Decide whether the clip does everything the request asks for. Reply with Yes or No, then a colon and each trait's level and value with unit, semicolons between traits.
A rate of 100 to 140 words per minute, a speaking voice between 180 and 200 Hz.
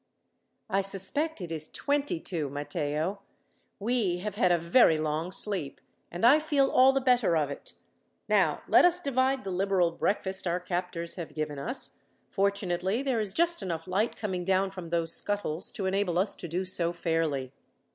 No: average, 175 wpm; high, 190 Hz